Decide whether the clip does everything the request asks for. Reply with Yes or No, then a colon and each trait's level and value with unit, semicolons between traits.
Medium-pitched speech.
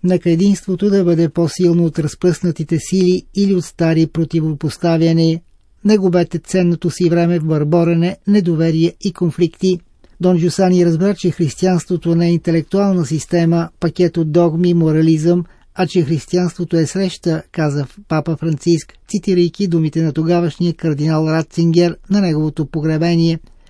Yes: medium, 170 Hz